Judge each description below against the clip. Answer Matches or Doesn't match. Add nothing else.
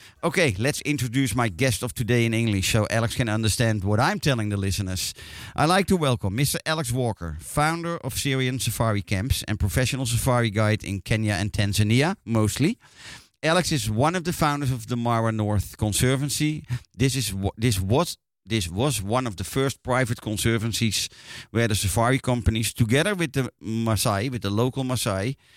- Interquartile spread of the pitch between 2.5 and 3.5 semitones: Doesn't match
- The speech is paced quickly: Doesn't match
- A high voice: Doesn't match